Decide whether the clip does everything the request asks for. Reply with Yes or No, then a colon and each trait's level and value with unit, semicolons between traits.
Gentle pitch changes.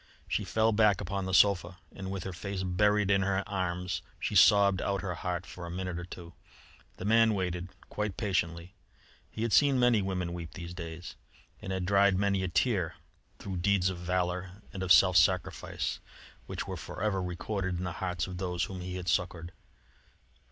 Yes: narrow, 1.9 semitones